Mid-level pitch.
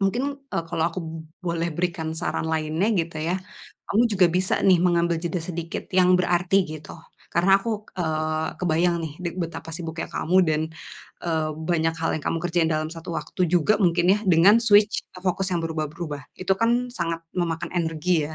Yes: medium, 170 Hz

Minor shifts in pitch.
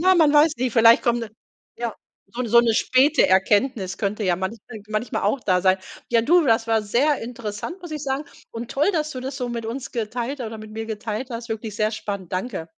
No: average, 3.9 semitones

